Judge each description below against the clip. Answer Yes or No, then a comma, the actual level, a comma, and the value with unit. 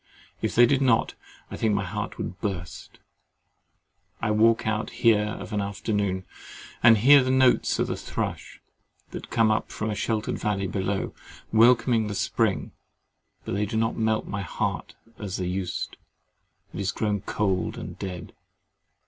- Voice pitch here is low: Yes, low, 105 Hz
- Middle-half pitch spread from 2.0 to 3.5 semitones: Yes, narrow, 2.5 semitones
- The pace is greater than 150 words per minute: Yes, average, 165 wpm